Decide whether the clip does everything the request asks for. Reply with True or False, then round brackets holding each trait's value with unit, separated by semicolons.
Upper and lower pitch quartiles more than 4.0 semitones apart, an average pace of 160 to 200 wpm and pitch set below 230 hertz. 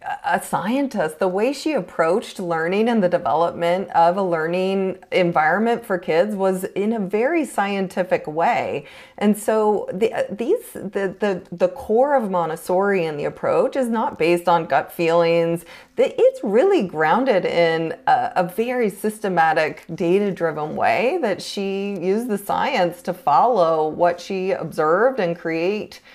False (4.6 semitones; 145 wpm; 190 Hz)